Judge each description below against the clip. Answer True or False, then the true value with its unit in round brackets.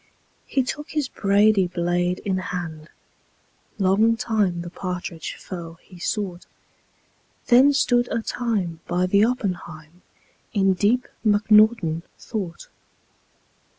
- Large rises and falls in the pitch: False (4.0 semitones)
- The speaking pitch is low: False (195 Hz)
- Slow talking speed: True (110 wpm)